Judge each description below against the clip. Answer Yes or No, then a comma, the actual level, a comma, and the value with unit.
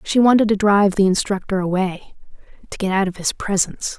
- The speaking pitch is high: Yes, high, 195 Hz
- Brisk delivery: No, average, 195 wpm